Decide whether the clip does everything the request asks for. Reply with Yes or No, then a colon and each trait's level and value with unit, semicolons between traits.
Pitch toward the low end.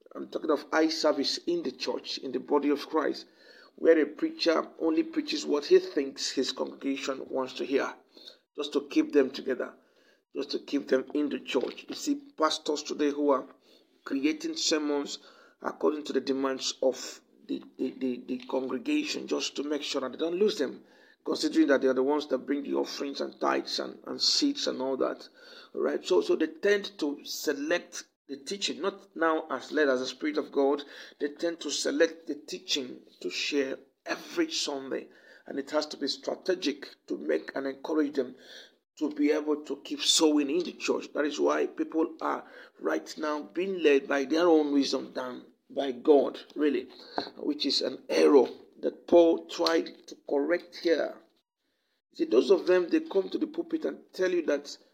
No: medium, 160 Hz